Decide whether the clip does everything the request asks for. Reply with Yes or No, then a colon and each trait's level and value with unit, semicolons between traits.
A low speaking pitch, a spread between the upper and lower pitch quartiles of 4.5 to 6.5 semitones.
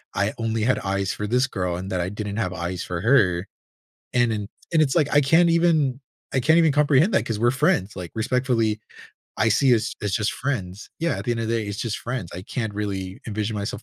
Yes: low, 110 Hz; average, 5.2 semitones